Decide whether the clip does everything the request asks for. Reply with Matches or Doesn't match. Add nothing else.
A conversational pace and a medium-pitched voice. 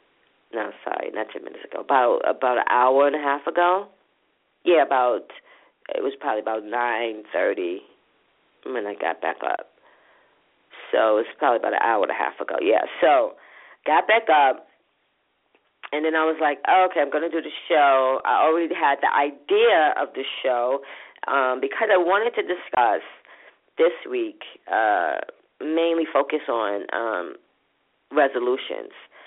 Matches